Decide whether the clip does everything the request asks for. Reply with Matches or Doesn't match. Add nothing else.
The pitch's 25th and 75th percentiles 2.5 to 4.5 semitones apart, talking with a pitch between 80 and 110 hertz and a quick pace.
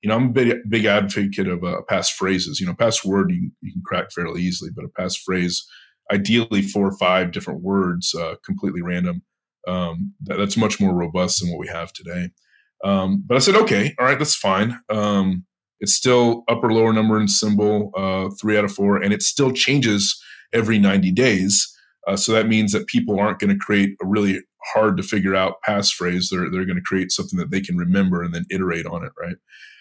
Matches